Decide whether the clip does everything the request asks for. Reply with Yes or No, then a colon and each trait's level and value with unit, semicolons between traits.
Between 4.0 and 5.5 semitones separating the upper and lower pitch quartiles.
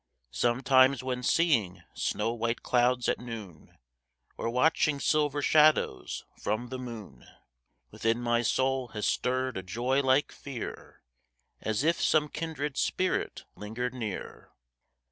No: average, 3.2 semitones